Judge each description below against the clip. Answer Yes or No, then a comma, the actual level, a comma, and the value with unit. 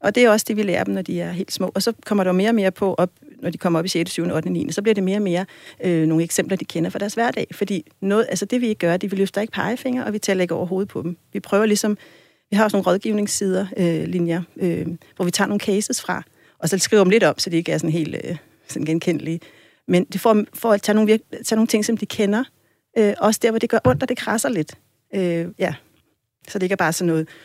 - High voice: Yes, high, 195 Hz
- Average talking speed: No, fast, 290 wpm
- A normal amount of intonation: Yes, average, 3.7 semitones